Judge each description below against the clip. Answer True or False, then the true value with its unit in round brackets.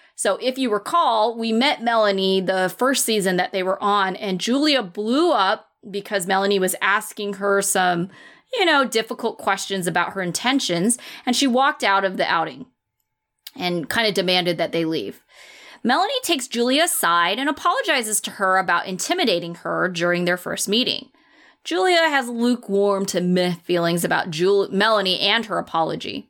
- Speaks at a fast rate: False (165 wpm)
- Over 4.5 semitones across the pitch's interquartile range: True (5.2 semitones)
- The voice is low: False (205 Hz)